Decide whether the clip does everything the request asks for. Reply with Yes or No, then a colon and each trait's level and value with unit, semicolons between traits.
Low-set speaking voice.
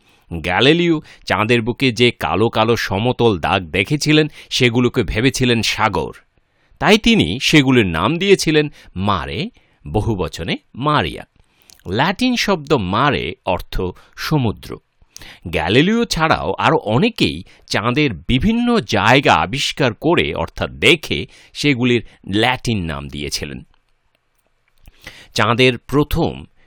Yes: low, 120 Hz